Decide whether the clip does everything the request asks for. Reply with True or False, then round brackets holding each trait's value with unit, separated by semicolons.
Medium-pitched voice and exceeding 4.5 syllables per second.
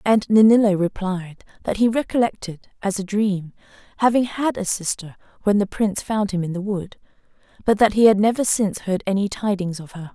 False (200 Hz; 5.4 syllables/s)